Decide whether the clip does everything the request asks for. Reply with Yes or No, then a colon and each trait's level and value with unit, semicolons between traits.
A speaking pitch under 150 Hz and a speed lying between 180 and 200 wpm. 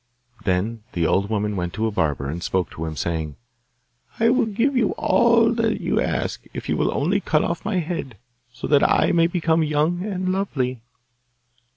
Yes: medium, 140 Hz; average, 185 wpm